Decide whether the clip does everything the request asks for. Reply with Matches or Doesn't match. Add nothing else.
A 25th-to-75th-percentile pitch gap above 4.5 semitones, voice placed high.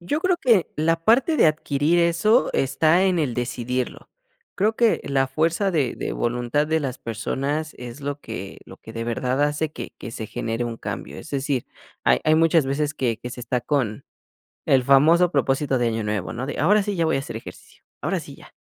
Doesn't match